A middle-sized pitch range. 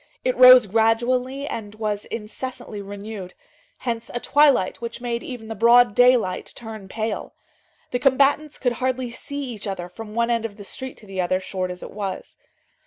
Yes: average, 3.6 semitones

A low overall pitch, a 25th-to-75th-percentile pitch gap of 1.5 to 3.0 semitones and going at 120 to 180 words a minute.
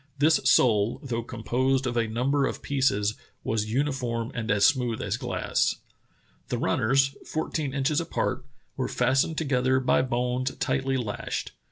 Yes: low, 130 Hz; average, 2.7 semitones; average, 145 wpm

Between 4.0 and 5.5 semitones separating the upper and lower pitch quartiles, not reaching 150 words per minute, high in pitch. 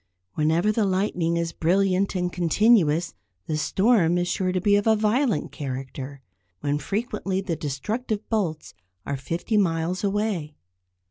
No: average, 4.5 semitones; average, 140 wpm; medium, 180 Hz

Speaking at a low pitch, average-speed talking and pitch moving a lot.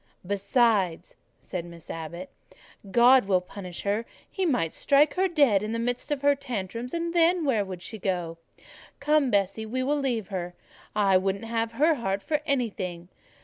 No: high, 225 Hz; average, 170 wpm; wide, 6.6 semitones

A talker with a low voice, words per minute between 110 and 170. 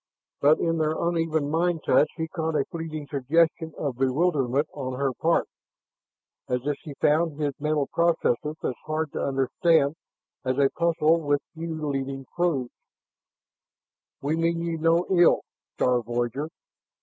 No: medium, 155 Hz; average, 145 wpm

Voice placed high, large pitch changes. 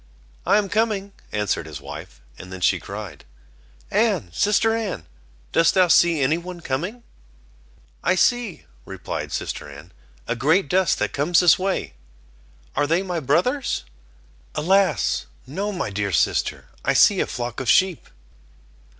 No: medium, 170 Hz; wide, 8.5 semitones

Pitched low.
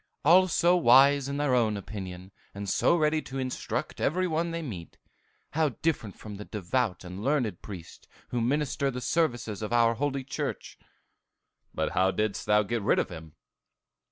Yes: low, 120 Hz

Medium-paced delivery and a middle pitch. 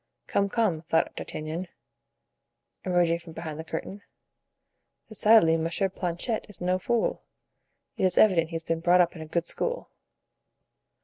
Yes: average, 145 wpm; medium, 175 Hz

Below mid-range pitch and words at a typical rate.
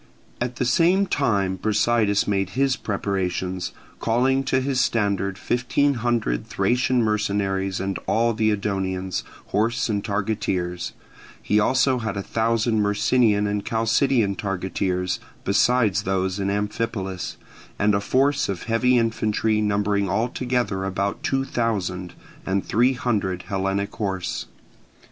No: low, 105 Hz; slow, 125 wpm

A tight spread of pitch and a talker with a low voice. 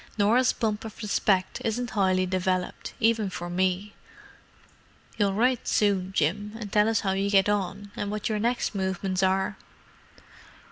No: narrow, 2.1 semitones; high, 200 Hz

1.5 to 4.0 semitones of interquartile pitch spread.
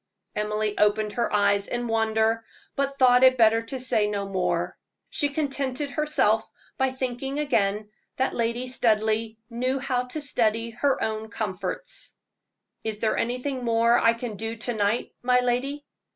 Yes: average, 3.0 semitones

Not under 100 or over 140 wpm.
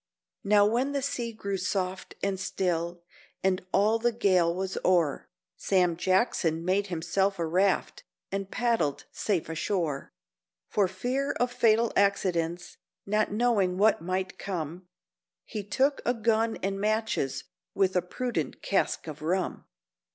Yes: slow, 135 wpm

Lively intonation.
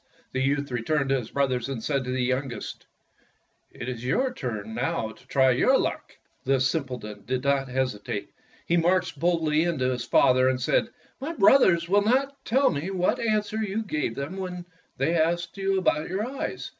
Yes: wide, 6.6 semitones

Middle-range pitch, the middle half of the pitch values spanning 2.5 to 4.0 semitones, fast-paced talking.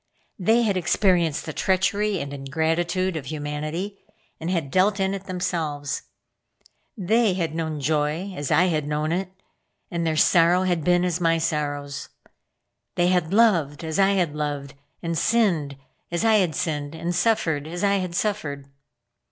No: medium, 170 Hz; average, 3.7 semitones; average, 160 wpm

